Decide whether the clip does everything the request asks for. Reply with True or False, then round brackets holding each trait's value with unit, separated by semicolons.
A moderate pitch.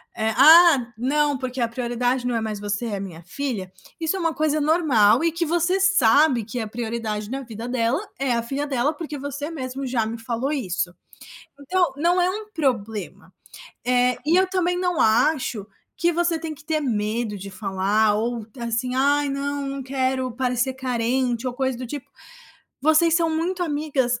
False (260 Hz)